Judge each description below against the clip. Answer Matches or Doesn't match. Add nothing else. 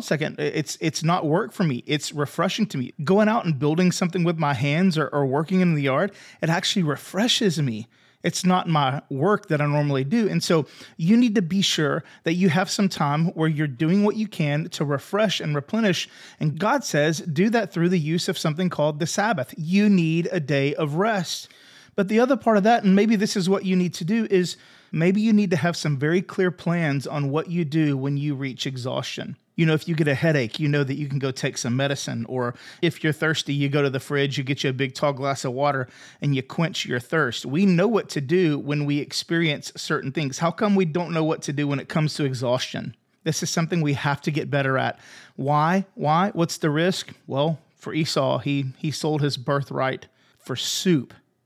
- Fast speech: Matches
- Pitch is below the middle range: Doesn't match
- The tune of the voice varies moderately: Matches